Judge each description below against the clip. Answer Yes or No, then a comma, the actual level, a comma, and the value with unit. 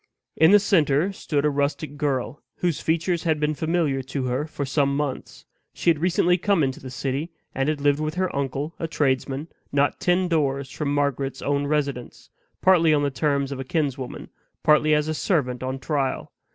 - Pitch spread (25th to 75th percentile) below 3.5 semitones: Yes, average, 2.7 semitones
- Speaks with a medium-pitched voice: Yes, medium, 145 Hz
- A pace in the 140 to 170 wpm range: No, average, 190 wpm